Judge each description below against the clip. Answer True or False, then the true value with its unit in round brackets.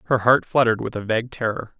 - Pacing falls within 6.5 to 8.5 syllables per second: True (7.0 syllables/s)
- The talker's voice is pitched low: True (115 Hz)